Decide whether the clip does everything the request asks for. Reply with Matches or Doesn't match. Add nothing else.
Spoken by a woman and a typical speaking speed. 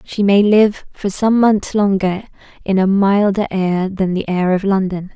Matches